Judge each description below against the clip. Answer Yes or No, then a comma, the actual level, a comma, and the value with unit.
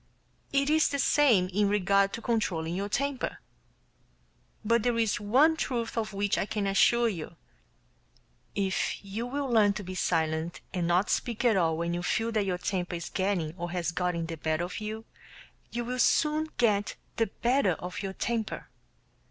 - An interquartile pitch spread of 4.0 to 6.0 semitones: Yes, average, 4.8 semitones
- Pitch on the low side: No, high, 205 Hz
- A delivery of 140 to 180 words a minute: Yes, average, 175 wpm